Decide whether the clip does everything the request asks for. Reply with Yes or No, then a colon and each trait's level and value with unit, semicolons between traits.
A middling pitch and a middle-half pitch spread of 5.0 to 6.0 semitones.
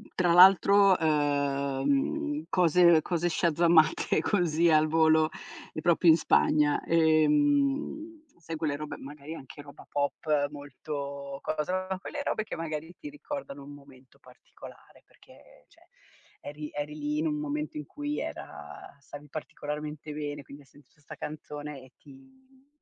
Yes: medium, 155 Hz; average, 5.3 semitones